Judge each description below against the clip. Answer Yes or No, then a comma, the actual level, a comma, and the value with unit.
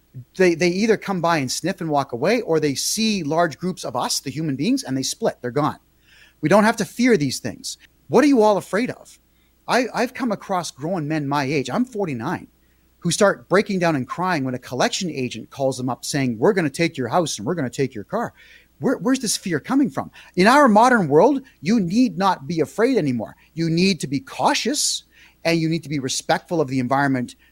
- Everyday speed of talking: No, fast, 230 wpm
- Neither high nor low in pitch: Yes, medium, 165 Hz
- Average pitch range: No, wide, 6.6 semitones